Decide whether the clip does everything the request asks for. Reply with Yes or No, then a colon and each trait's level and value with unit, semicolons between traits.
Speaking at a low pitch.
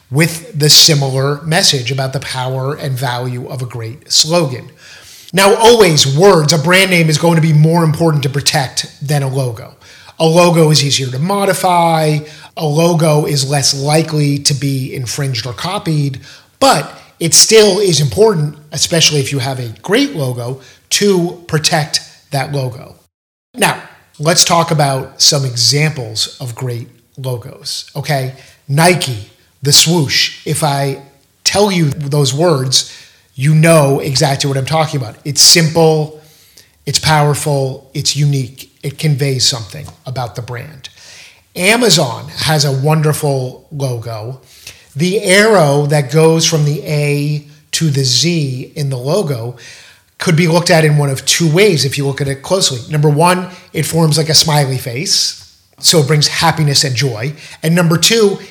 No: medium, 145 Hz